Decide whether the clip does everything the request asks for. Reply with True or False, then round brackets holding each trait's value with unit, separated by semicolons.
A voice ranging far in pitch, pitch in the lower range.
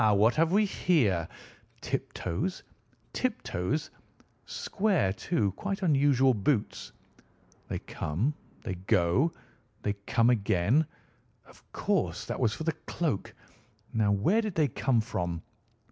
True (8.4 semitones; 120 Hz)